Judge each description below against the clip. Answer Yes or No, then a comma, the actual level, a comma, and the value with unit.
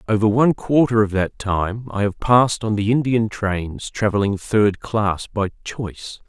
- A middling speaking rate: Yes, average, 170 wpm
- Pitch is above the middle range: No, low, 105 Hz